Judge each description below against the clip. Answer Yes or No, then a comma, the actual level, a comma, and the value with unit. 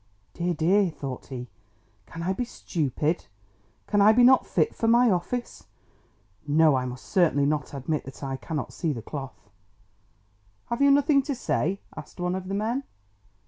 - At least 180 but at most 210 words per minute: No, average, 170 wpm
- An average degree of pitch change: No, wide, 7.5 semitones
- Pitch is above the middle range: No, medium, 175 Hz